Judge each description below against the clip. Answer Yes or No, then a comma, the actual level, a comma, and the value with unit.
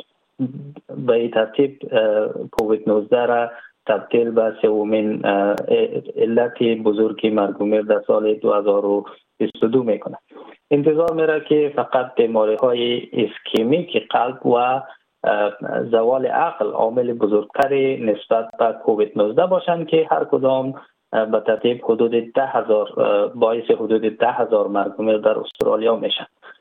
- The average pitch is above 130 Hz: No, low, 120 Hz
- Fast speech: No, average, 110 wpm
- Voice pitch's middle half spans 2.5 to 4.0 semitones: No, average, 5.2 semitones